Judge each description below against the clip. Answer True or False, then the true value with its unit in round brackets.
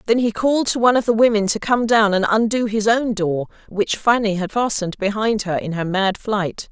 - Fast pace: True (230 wpm)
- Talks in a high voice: True (215 Hz)